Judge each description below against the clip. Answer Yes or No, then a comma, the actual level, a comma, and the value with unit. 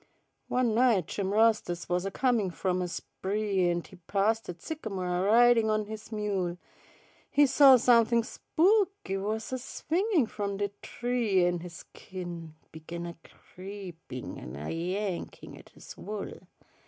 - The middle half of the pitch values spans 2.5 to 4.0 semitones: No, average, 4.5 semitones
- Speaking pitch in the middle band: No, high, 205 Hz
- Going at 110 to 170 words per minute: Yes, average, 150 wpm